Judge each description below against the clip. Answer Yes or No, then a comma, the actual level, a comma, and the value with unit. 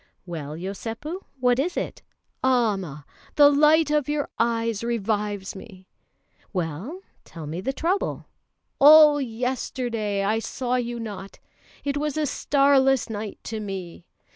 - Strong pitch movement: Yes, wide, 6.1 semitones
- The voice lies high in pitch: Yes, high, 230 Hz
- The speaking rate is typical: No, slow, 130 wpm